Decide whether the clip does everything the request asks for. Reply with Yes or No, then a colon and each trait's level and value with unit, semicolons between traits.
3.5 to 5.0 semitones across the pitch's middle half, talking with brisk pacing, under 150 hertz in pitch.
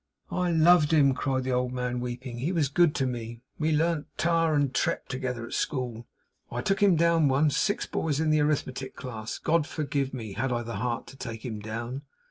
Yes: average, 4.2 semitones; fast, 210 wpm; low, 135 Hz